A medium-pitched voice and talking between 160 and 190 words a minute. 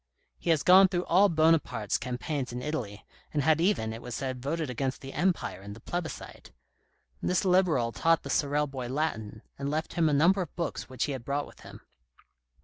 No: medium, 145 Hz; average, 200 wpm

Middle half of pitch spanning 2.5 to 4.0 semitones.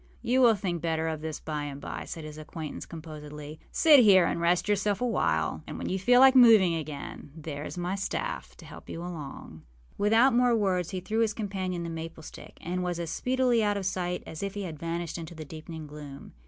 No: average, 4.7 semitones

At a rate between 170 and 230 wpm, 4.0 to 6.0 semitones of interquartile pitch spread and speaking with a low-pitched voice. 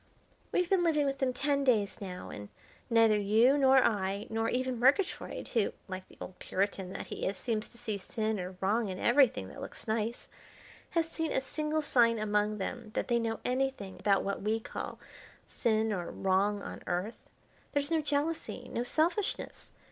No: average, 180 wpm; average, 4.9 semitones; high, 230 Hz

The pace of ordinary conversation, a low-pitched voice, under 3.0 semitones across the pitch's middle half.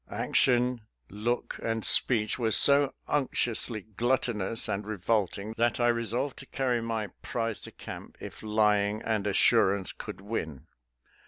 Yes: average, 145 wpm; low, 115 Hz; narrow, 2.5 semitones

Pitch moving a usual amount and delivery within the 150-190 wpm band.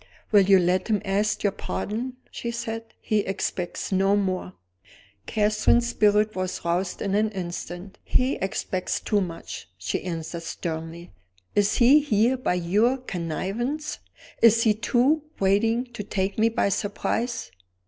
No: average, 3.6 semitones; average, 140 wpm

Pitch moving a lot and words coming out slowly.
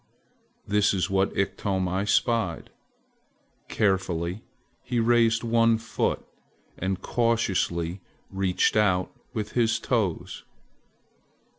No: average, 3.5 semitones; slow, 90 wpm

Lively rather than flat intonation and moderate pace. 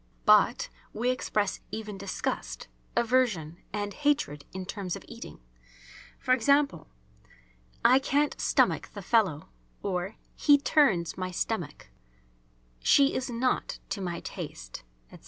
No: wide, 6.2 semitones; slow, 120 wpm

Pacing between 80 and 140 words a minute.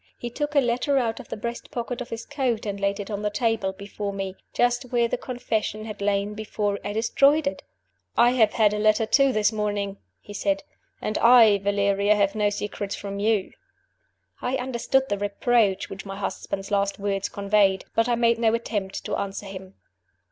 No: average, 195 wpm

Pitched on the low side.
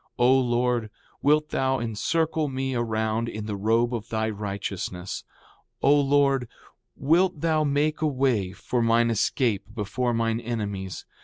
Yes: low, 120 Hz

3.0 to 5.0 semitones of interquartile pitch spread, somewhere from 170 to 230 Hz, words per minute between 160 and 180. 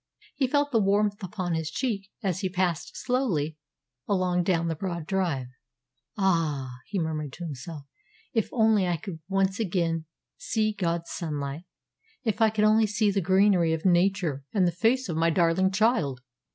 Yes: average, 4.0 semitones; medium, 185 Hz; average, 165 wpm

